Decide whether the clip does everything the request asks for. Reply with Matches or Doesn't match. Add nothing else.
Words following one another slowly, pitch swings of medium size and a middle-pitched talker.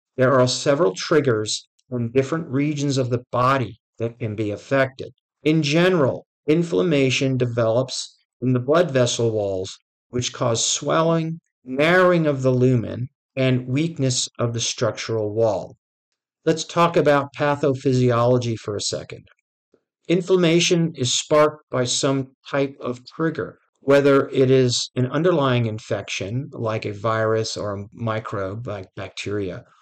Doesn't match